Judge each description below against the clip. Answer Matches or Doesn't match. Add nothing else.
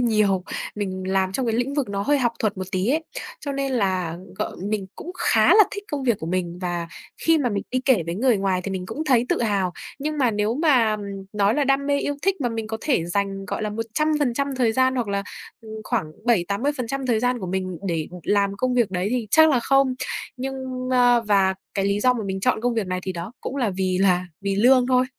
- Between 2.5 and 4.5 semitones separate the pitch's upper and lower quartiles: Doesn't match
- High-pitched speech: Matches